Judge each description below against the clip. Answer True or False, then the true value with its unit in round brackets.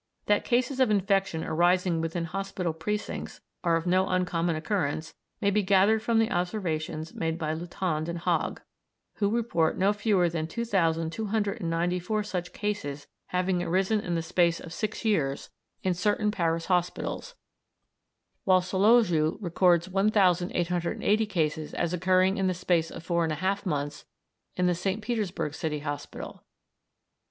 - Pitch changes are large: False (3.4 semitones)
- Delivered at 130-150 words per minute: True (145 wpm)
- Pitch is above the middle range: False (180 Hz)